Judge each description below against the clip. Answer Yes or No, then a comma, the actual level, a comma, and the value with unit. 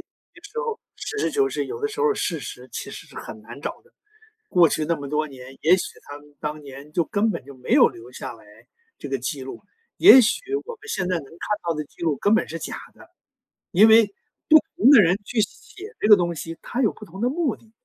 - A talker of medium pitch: Yes, medium, 175 Hz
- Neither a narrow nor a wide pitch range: No, wide, 9.0 semitones